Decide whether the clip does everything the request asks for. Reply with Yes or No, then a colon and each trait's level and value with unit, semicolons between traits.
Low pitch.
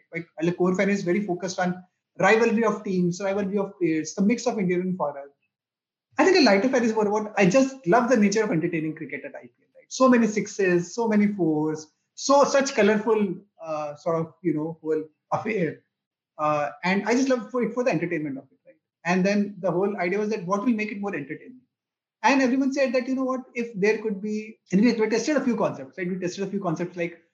No: high, 200 Hz